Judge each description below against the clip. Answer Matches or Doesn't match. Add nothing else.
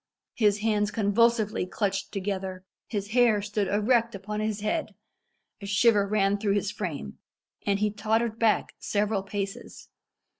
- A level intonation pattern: Matches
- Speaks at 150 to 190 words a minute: Doesn't match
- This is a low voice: Doesn't match